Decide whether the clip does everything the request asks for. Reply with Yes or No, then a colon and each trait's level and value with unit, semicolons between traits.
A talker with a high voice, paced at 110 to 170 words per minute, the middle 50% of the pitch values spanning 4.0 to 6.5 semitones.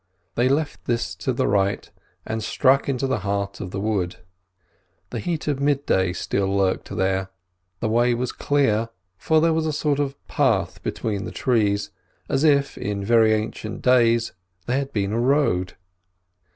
No: low, 115 Hz; average, 165 wpm; wide, 5.6 semitones